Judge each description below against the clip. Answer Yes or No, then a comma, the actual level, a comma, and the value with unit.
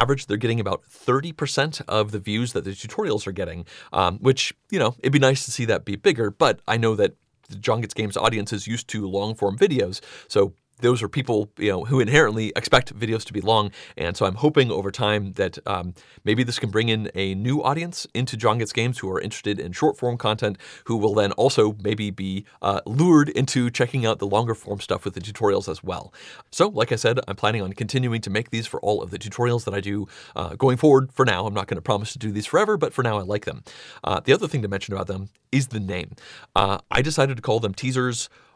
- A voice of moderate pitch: No, low, 110 Hz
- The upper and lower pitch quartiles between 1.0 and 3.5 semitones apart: No, average, 3.9 semitones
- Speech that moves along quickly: Yes, fast, 240 wpm